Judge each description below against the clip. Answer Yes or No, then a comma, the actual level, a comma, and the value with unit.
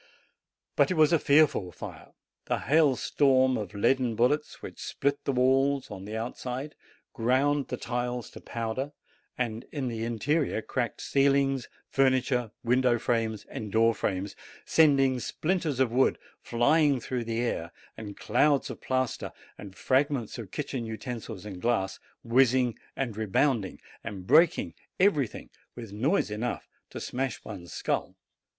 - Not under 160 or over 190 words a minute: No, average, 140 wpm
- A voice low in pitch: Yes, low, 125 Hz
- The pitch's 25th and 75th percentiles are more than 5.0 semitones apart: No, average, 3.6 semitones